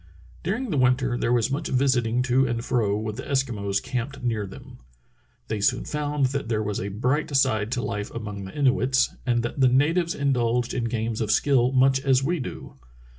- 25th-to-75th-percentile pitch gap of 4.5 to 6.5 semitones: No, average, 3.1 semitones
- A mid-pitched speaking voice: No, low, 125 Hz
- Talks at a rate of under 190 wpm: No, average, 200 wpm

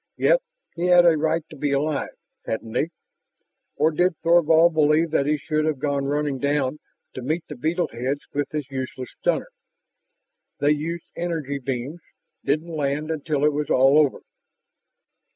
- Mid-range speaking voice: Yes, medium, 150 Hz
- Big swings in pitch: No, narrow, 2.6 semitones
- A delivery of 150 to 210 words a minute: Yes, average, 160 wpm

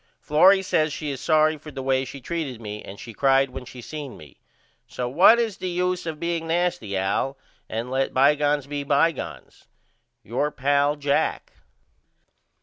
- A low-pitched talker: No, medium, 145 Hz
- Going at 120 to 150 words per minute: No, average, 170 wpm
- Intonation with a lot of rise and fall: No, average, 3.6 semitones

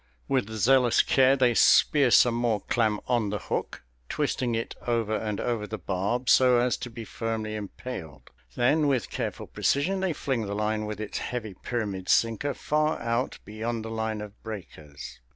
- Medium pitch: No, low, 115 Hz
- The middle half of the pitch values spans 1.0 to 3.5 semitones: Yes, average, 2.8 semitones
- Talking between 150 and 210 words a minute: Yes, average, 170 wpm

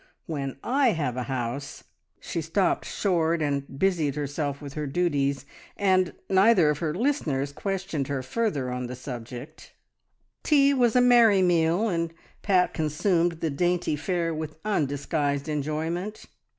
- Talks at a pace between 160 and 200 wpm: No, average, 145 wpm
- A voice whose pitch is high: No, medium, 160 Hz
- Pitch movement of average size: Yes, average, 4.8 semitones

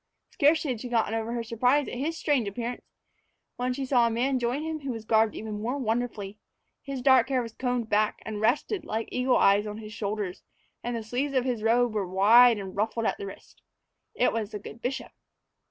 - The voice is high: Yes, high, 235 Hz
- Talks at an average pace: No, fast, 215 wpm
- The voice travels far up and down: No, average, 3.0 semitones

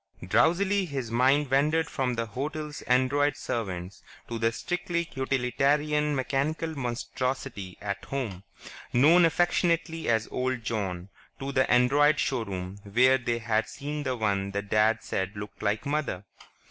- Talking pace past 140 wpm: No, slow, 135 wpm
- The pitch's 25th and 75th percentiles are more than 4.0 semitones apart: Yes, average, 5.1 semitones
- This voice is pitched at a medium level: No, low, 130 Hz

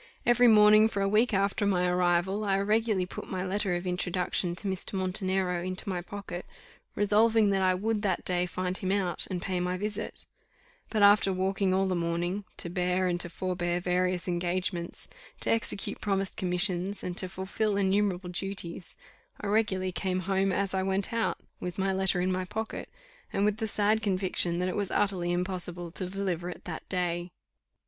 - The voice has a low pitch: No, high, 190 Hz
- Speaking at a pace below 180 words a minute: No, average, 185 wpm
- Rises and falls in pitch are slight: Yes, narrow, 2.0 semitones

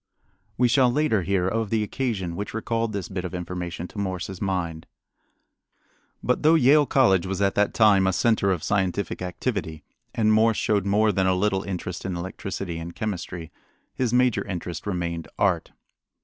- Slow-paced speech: No, average, 170 wpm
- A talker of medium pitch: No, very low, 95 Hz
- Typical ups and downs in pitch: Yes, average, 3.6 semitones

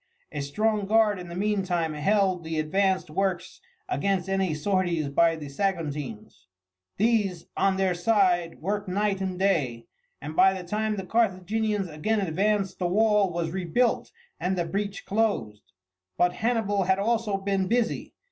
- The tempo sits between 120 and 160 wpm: Yes, average, 150 wpm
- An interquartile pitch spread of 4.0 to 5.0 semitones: No, average, 3.3 semitones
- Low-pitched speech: No, high, 190 Hz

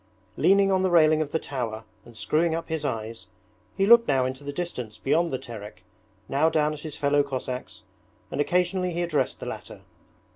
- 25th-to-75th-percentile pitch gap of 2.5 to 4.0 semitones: No, average, 5.0 semitones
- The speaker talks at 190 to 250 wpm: Yes, average, 195 wpm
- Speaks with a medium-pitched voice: Yes, medium, 150 Hz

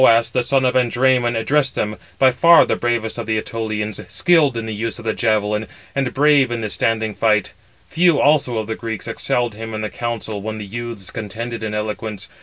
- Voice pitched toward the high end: No, low, 115 Hz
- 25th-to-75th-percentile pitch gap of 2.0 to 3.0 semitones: Yes, narrow, 2.5 semitones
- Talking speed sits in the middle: No, fast, 210 wpm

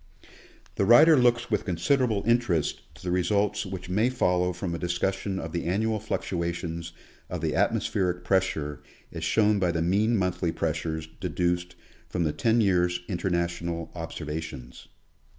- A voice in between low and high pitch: No, very low, 90 Hz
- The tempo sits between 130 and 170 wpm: Yes, average, 145 wpm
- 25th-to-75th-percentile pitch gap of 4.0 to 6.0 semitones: No, average, 3.4 semitones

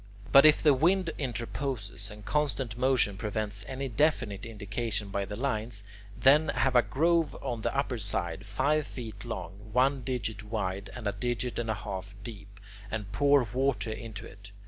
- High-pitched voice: No, low, 115 Hz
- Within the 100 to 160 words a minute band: No, average, 170 wpm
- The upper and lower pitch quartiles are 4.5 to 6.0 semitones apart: Yes, average, 4.8 semitones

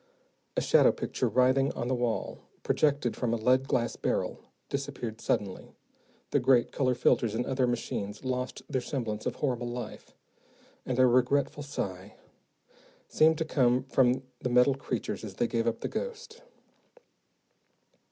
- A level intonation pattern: Yes, narrow, 2.2 semitones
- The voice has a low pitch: Yes, low, 125 Hz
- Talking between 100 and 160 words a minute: Yes, average, 150 wpm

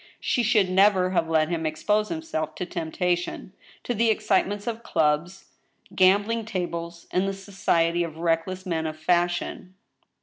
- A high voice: No, medium, 180 Hz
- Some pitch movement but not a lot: Yes, average, 3.3 semitones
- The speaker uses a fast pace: No, average, 145 wpm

